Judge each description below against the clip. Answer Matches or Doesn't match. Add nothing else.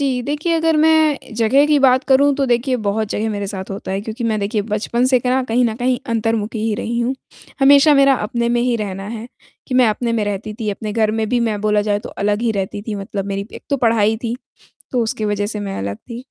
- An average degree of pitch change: Matches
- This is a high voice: Matches